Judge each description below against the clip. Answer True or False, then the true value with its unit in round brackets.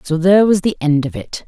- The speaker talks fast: True (285 wpm)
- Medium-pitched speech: True (175 Hz)